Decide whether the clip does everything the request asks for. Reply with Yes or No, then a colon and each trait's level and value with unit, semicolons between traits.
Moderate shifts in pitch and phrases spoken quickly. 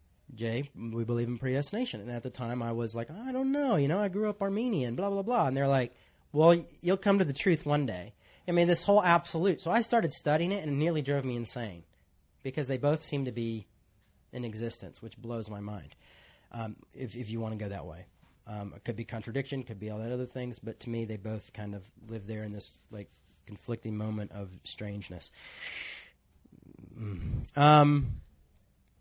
No: wide, 6.0 semitones; fast, 210 wpm